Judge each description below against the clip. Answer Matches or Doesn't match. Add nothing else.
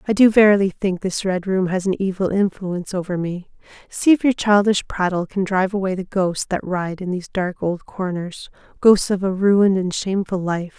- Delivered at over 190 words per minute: Matches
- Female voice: Matches